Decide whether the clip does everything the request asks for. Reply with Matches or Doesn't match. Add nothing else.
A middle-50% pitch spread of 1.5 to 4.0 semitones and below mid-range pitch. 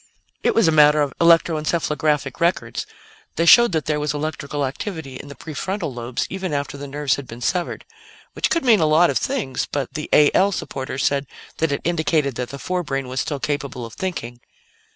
Doesn't match